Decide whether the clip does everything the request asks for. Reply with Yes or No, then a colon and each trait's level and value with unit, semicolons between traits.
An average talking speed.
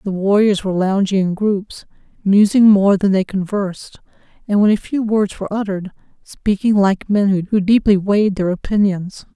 Yes: average, 165 wpm